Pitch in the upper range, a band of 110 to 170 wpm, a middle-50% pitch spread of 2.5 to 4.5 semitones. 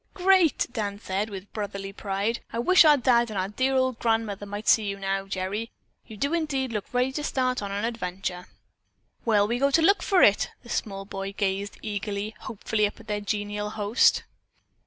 No: high, 210 Hz; average, 190 wpm; average, 3.9 semitones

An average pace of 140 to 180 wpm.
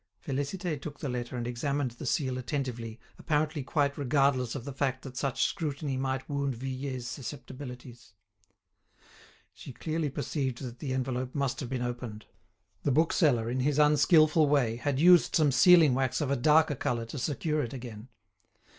Yes: average, 165 wpm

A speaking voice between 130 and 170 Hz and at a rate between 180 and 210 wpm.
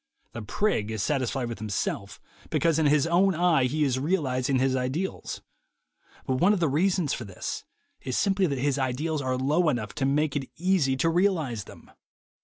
Yes: medium, 140 Hz; average, 185 wpm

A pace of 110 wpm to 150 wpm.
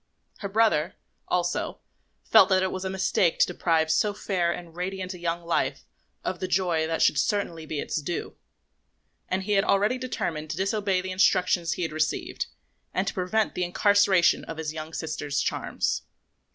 No: average, 180 wpm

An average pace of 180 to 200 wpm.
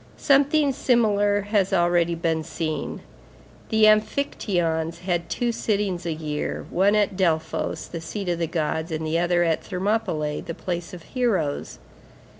No: average, 140 wpm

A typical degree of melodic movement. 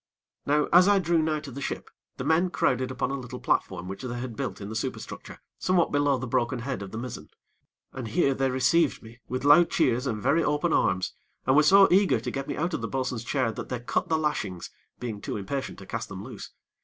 Yes: average, 4.4 semitones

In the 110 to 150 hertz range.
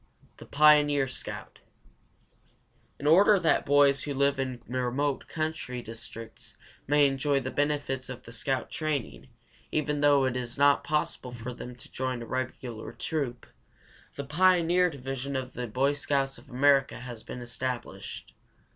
Yes: low, 135 Hz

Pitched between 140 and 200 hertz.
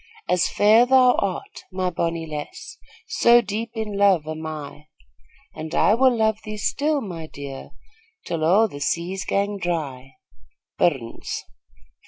Yes: medium, 185 Hz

